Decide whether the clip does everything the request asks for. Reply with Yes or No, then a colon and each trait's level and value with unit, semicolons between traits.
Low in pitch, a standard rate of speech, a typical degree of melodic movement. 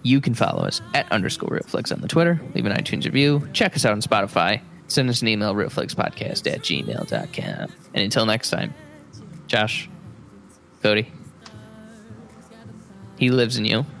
No: low, 125 Hz; average, 155 wpm; wide, 6.3 semitones